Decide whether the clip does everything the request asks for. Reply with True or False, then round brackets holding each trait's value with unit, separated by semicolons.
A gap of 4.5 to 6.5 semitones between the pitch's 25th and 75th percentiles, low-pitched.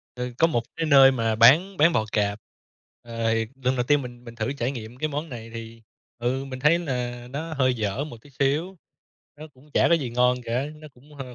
False (3.8 semitones; 130 Hz)